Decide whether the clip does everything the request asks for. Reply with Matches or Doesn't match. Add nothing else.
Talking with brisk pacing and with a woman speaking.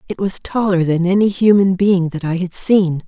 Matches